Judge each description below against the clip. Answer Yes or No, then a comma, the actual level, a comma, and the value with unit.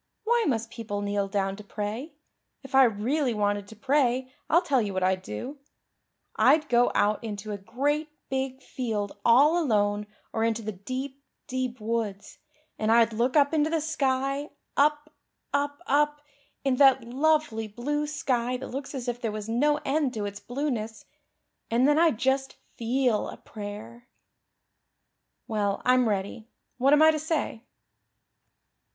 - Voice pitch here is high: Yes, very high, 250 Hz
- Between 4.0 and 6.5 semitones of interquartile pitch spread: Yes, average, 4.8 semitones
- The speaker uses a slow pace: No, average, 160 wpm